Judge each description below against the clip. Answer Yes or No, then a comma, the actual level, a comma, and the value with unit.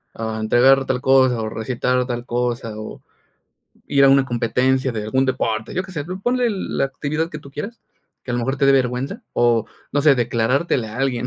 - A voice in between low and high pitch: No, low, 130 Hz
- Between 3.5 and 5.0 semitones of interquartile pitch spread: No, narrow, 2.6 semitones